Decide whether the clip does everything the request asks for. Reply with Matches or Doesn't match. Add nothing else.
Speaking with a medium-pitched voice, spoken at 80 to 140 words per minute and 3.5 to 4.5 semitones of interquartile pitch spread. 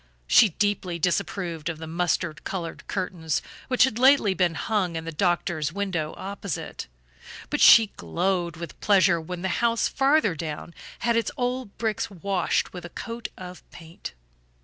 Doesn't match